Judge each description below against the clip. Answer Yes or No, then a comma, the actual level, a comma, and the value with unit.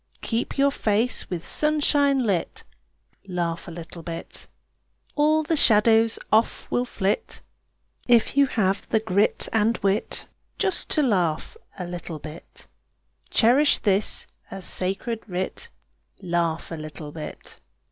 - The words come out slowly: Yes, slow, 125 wpm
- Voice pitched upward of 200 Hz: Yes, high, 210 Hz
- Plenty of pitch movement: Yes, wide, 6.0 semitones